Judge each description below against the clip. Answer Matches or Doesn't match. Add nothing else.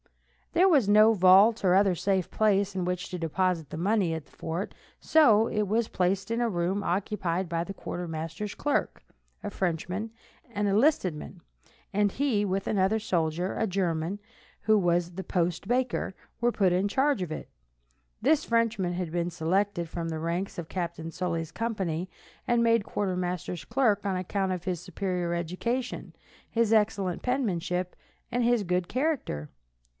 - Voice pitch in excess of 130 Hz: Matches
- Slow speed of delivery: Doesn't match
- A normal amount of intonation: Matches